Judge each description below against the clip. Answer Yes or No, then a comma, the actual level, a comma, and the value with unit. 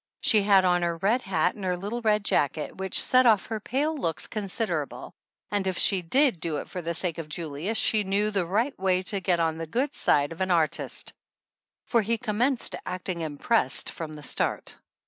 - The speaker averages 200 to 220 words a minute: Yes, fast, 205 wpm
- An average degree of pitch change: Yes, average, 4.5 semitones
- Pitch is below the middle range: No, high, 190 Hz